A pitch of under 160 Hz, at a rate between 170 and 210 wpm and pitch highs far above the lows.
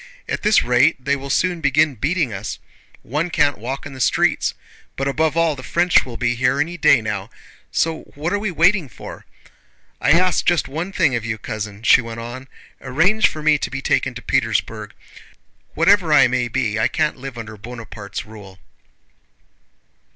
Yes: low, 135 Hz; average, 180 wpm; wide, 5.8 semitones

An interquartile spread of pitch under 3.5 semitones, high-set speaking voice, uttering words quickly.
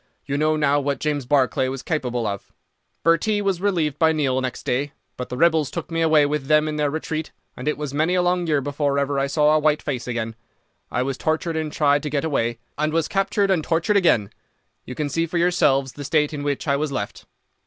No: average, 2.7 semitones; medium, 150 Hz; fast, 230 wpm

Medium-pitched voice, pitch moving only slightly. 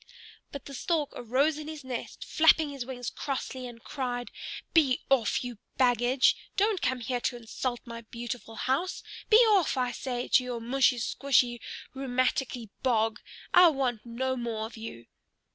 No: very high, 250 Hz; narrow, 2.3 semitones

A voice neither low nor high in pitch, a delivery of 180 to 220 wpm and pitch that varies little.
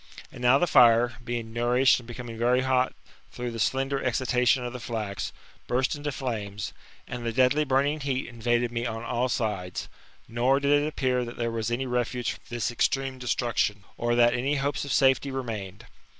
No: low, 125 Hz; average, 190 wpm; narrow, 2.0 semitones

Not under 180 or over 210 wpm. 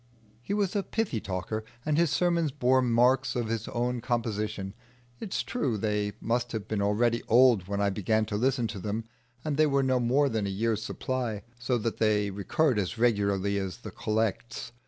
Yes: average, 195 wpm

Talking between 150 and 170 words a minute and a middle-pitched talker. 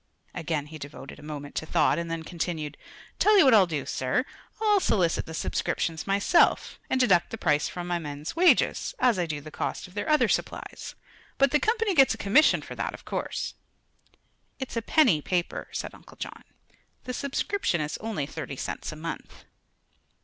No: average, 185 wpm; medium, 175 Hz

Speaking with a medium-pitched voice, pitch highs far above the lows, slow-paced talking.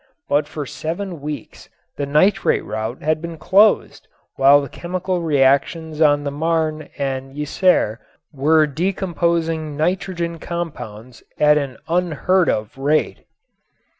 No: medium, 155 Hz; average, 3.3 semitones; slow, 120 wpm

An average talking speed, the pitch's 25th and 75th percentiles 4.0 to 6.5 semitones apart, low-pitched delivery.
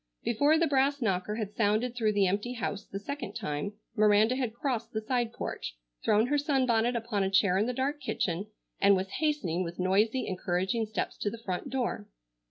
No: average, 190 wpm; average, 4.3 semitones; high, 220 Hz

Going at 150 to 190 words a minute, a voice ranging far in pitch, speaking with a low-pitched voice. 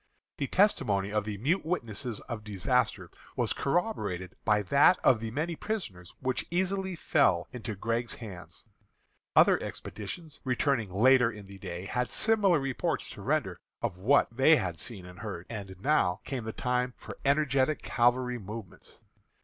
Yes: average, 155 wpm; wide, 6.1 semitones; low, 120 Hz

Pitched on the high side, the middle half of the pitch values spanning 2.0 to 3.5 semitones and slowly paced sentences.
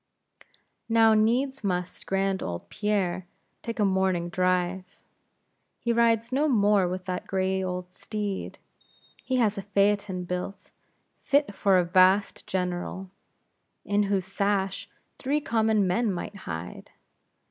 Yes: high, 195 Hz; average, 2.8 semitones; slow, 125 wpm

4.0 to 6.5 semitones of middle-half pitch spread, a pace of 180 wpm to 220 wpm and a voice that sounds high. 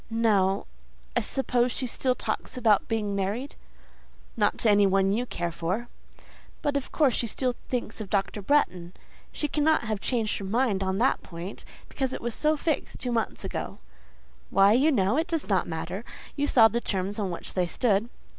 Yes: average, 4.6 semitones; average, 185 wpm; high, 220 Hz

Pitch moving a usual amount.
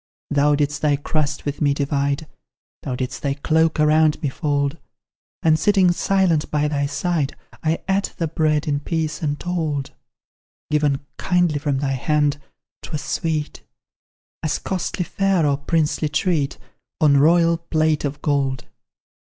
No: narrow, 2.3 semitones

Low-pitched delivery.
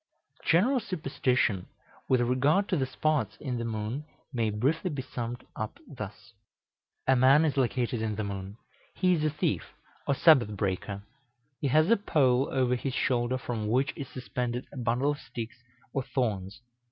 Yes: low, 125 Hz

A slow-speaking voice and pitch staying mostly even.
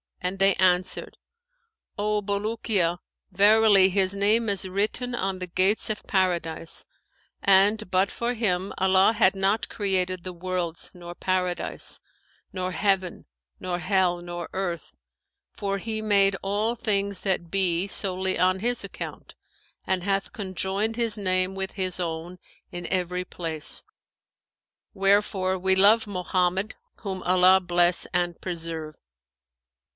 Yes: slow, 130 wpm; narrow, 2.0 semitones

